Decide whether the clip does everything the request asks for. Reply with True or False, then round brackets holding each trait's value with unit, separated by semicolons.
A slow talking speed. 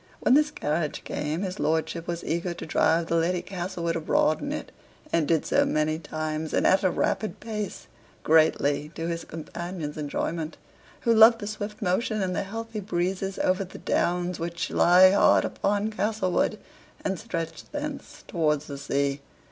False (165 wpm)